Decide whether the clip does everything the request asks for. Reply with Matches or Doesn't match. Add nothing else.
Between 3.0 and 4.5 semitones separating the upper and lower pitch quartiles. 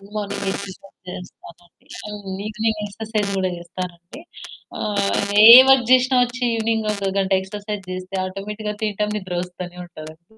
Doesn't match